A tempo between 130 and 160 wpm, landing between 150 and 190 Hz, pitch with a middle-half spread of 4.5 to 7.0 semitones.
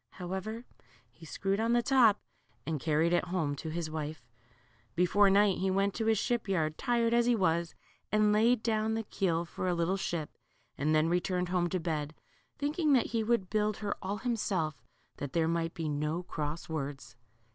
No: average, 190 wpm; medium, 185 Hz; average, 5.1 semitones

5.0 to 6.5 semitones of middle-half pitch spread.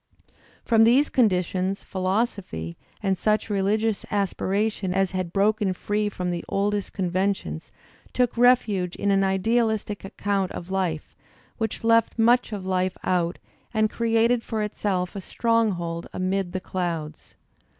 No: average, 3.0 semitones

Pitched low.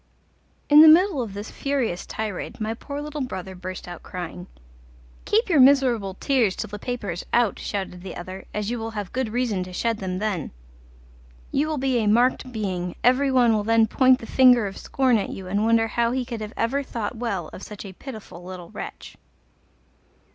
No: high, 225 Hz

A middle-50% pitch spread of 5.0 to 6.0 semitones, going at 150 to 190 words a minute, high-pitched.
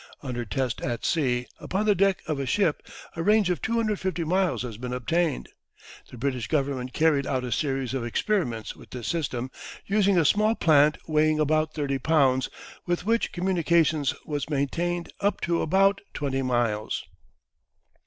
No: wide, 5.4 semitones; average, 160 wpm; medium, 155 Hz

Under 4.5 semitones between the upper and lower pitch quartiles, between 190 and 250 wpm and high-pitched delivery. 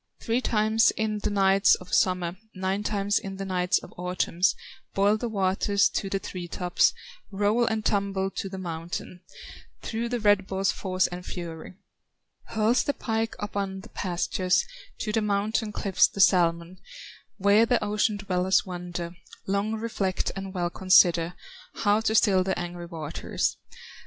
No: narrow, 2.6 semitones; average, 155 wpm; high, 195 Hz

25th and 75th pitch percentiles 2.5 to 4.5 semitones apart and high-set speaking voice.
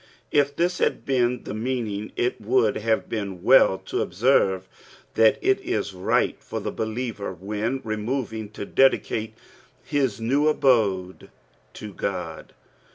No: average, 4.0 semitones; low, 115 Hz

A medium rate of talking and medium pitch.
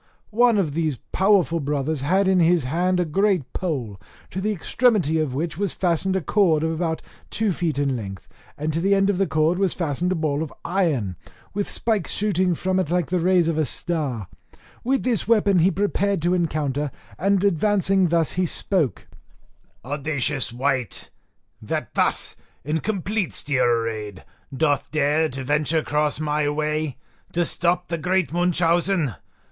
Yes: average, 170 wpm; medium, 165 Hz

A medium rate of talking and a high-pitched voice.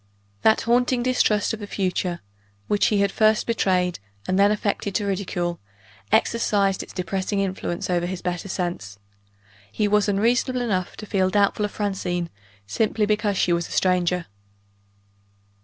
Yes: average, 150 wpm; high, 200 Hz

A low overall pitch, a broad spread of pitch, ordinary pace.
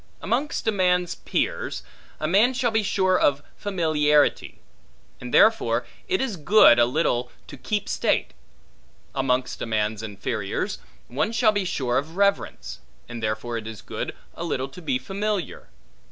No: medium, 155 Hz; wide, 8.9 semitones; average, 155 wpm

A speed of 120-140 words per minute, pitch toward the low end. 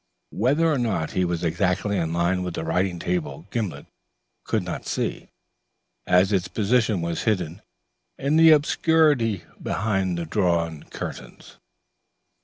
Yes: slow, 135 wpm; very low, 95 Hz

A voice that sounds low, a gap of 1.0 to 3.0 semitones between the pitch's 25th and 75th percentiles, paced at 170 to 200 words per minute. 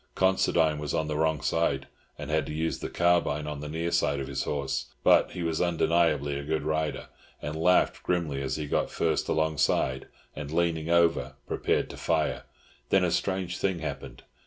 Yes: very low, 80 Hz; average, 2.7 semitones; average, 185 wpm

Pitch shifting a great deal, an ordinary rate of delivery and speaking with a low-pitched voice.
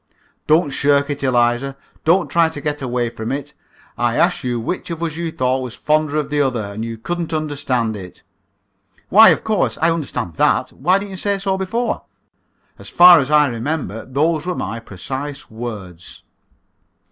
No: wide, 5.7 semitones; average, 180 wpm; medium, 145 Hz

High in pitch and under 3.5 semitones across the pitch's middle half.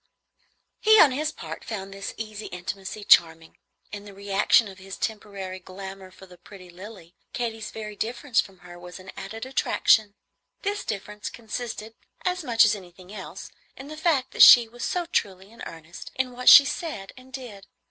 No: high, 205 Hz; average, 4.2 semitones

